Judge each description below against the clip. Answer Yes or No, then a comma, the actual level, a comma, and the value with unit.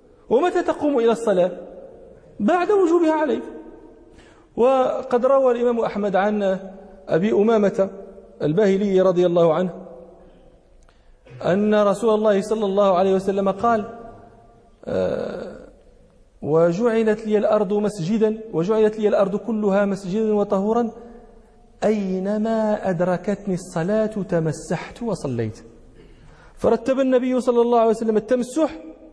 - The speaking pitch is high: Yes, high, 210 Hz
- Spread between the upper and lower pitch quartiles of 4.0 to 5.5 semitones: No, average, 3.5 semitones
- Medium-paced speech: No, slow, 100 wpm